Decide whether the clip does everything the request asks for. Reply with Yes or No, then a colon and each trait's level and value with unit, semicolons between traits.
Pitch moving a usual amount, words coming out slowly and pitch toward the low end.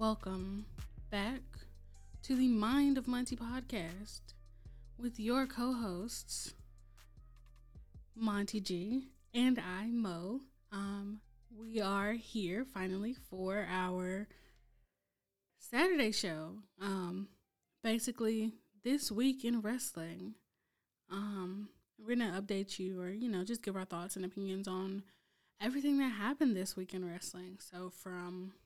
No: average, 4.3 semitones; slow, 120 wpm; high, 200 Hz